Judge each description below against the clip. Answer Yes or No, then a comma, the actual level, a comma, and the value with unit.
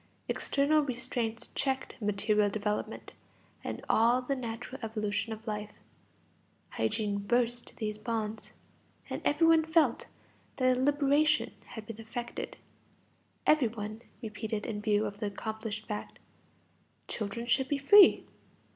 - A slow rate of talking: Yes, slow, 125 wpm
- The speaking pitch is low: No, high, 225 Hz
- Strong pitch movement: No, average, 3.7 semitones